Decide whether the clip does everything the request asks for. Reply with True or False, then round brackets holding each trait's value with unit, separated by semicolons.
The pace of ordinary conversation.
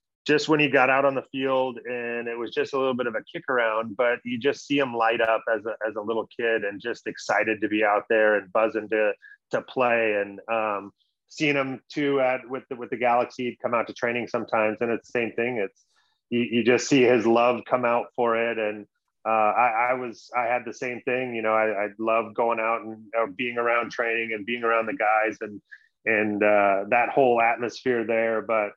False (230 wpm)